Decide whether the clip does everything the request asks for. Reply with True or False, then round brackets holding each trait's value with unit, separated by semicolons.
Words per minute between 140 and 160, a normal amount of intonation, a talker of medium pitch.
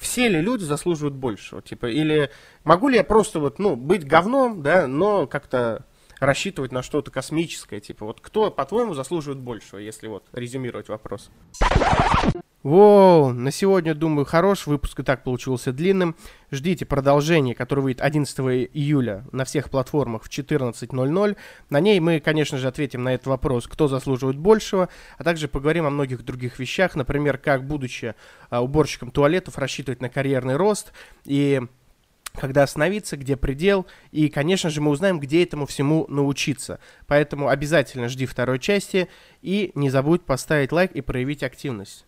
True (155 wpm; 4.1 semitones; 145 Hz)